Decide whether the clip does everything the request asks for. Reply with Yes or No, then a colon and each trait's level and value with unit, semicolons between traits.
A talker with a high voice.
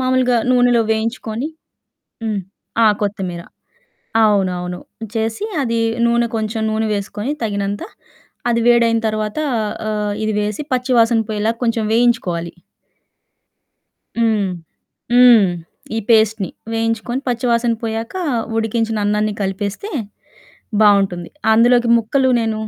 Yes: high, 225 Hz